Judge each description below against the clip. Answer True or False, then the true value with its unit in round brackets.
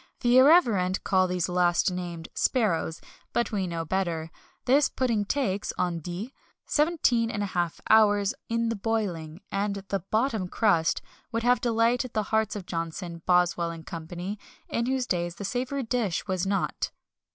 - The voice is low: False (200 Hz)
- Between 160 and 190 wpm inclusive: False (150 wpm)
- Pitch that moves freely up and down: False (4.7 semitones)